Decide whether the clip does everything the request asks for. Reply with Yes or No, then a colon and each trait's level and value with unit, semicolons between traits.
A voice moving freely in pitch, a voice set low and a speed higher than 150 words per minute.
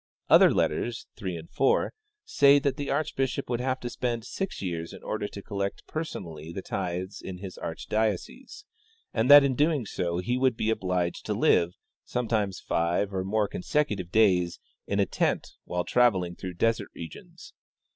Yes: wide, 5.7 semitones; low, 105 Hz; average, 175 wpm